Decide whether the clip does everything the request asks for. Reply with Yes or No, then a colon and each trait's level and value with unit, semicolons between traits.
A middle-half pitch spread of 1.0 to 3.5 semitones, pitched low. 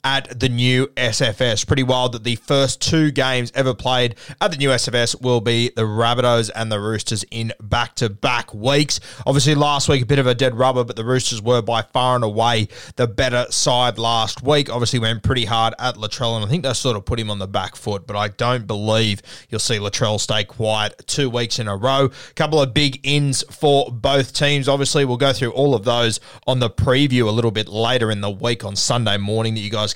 Yes: average, 3.1 semitones; low, 120 Hz